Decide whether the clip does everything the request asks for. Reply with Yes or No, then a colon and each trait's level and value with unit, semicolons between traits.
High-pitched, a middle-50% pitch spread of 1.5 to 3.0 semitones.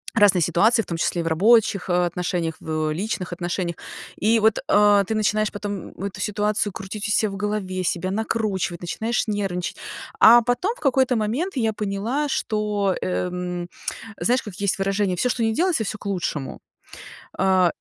No: high, 205 Hz; average, 3.5 semitones